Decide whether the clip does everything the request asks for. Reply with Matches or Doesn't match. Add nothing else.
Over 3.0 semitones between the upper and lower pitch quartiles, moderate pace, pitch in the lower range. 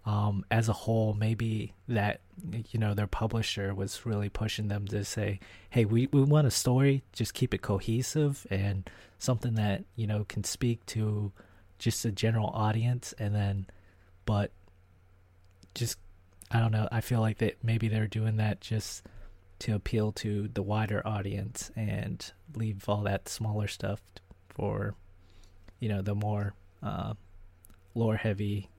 Doesn't match